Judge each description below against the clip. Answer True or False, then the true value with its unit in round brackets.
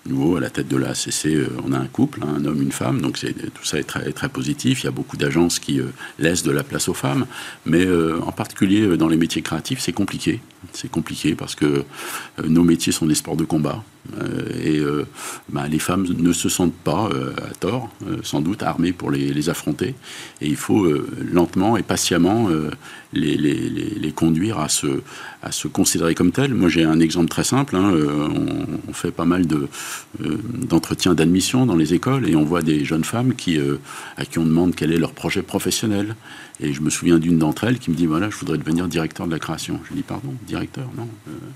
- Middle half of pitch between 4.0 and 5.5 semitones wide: False (2.9 semitones)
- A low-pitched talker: True (80 Hz)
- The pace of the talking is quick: True (235 wpm)